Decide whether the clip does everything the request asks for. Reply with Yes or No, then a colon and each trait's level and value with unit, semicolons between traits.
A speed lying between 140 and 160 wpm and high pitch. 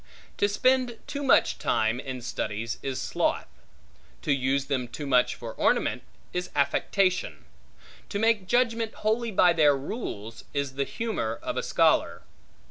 No: average, 145 wpm; medium, 150 Hz